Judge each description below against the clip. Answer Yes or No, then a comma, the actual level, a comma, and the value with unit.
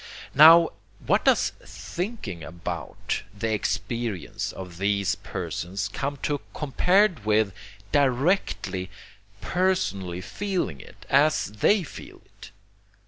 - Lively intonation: Yes, wide, 8.8 semitones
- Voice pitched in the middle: No, low, 110 Hz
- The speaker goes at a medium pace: No, slow, 100 wpm